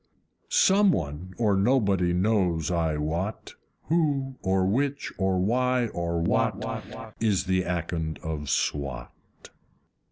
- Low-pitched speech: Yes, very low, 95 Hz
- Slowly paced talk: Yes, slow, 115 wpm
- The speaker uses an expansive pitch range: Yes, wide, 5.9 semitones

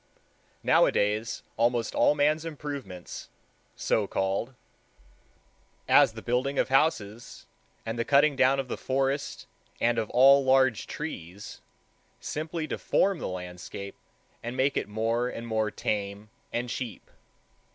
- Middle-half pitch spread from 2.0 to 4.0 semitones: No, average, 4.5 semitones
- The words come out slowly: Yes, slow, 125 wpm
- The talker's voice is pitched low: Yes, low, 120 Hz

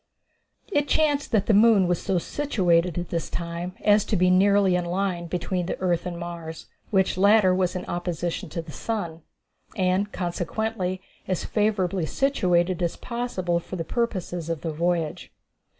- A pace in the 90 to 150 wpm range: No, average, 165 wpm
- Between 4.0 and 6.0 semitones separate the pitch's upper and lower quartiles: No, average, 2.9 semitones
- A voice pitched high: No, medium, 180 Hz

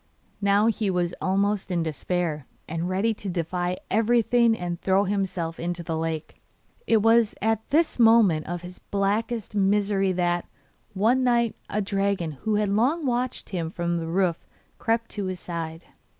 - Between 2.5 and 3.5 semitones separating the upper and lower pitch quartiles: No, average, 4.2 semitones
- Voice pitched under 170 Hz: No, high, 195 Hz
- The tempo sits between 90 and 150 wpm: No, average, 160 wpm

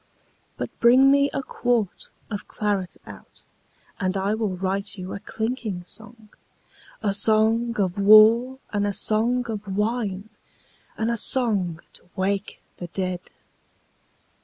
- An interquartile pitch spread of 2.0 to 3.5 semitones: Yes, average, 3.0 semitones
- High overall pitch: Yes, high, 210 Hz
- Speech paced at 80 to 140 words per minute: Yes, slow, 135 wpm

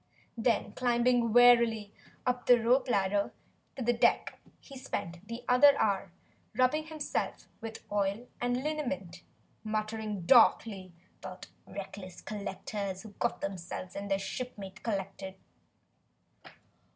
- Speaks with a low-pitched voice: No, high, 220 Hz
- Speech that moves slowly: Yes, slow, 115 wpm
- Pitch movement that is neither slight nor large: Yes, average, 3.9 semitones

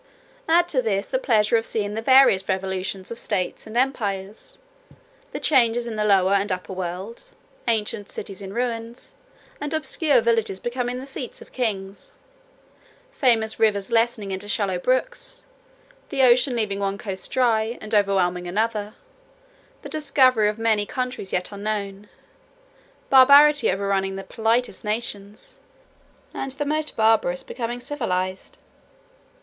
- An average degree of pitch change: Yes, average, 4.2 semitones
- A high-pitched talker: Yes, high, 220 Hz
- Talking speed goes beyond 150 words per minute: No, slow, 135 wpm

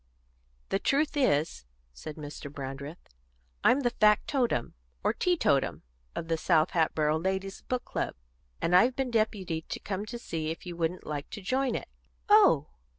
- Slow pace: No, average, 155 wpm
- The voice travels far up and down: Yes, wide, 7.5 semitones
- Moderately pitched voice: Yes, medium, 180 Hz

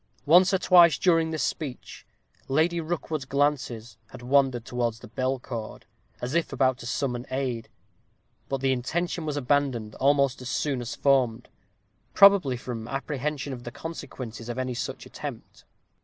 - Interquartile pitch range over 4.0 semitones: No, average, 3.6 semitones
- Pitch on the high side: No, low, 135 Hz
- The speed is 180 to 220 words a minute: No, average, 155 wpm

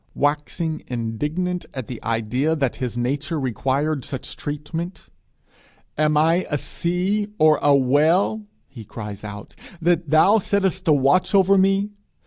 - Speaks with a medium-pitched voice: Yes, medium, 150 Hz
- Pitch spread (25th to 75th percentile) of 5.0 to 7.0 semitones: Yes, average, 5.3 semitones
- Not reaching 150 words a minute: Yes, slow, 135 wpm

